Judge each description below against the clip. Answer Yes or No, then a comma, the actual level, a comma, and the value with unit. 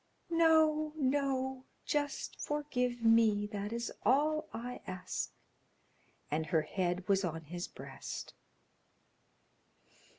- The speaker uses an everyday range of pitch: No, wide, 7.1 semitones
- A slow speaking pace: Yes, slow, 100 wpm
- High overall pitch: Yes, high, 240 Hz